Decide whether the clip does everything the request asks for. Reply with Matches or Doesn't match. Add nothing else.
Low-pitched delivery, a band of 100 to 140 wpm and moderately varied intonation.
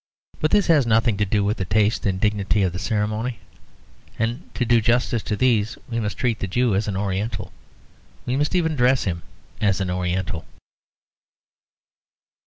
Doesn't match